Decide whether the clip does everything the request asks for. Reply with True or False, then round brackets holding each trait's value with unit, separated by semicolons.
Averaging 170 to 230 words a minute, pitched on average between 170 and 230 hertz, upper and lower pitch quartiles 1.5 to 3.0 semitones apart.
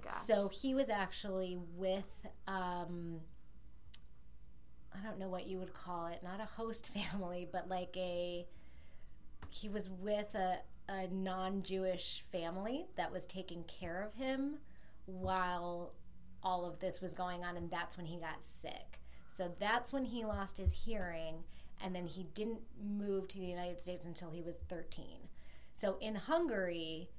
False (155 wpm; 185 Hz; 2.4 semitones)